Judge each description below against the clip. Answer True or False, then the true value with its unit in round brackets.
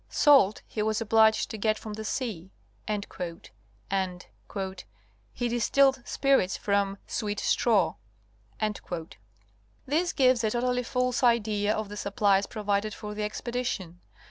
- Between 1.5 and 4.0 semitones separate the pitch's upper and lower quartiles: True (3.1 semitones)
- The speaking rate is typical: False (125 wpm)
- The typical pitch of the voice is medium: False (215 Hz)